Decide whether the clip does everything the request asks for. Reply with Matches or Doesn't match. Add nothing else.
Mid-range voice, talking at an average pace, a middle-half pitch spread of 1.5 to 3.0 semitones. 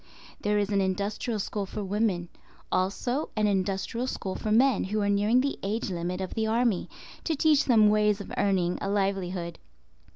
Doesn't match